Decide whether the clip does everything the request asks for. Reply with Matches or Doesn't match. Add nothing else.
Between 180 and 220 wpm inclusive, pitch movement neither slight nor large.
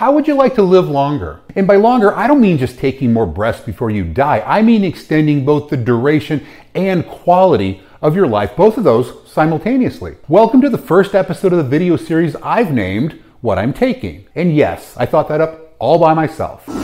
Doesn't match